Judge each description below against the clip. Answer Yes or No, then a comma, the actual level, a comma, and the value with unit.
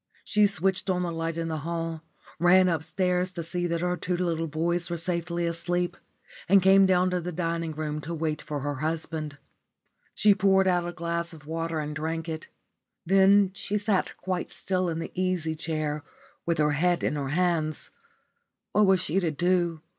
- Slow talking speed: No, average, 185 wpm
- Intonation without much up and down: Yes, narrow, 2.3 semitones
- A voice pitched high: No, medium, 170 Hz